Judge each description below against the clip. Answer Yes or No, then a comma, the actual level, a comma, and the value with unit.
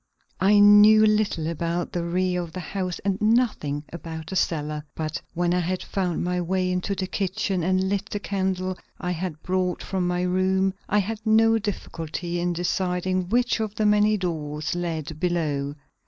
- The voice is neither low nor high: Yes, medium, 180 Hz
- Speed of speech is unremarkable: Yes, average, 175 wpm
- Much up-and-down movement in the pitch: No, average, 2.7 semitones